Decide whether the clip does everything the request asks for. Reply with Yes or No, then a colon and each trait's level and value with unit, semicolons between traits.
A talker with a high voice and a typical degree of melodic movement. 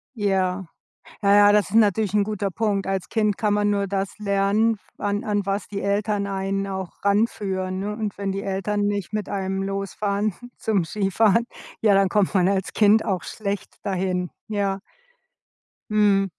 No: high, 200 Hz; narrow, 1.3 semitones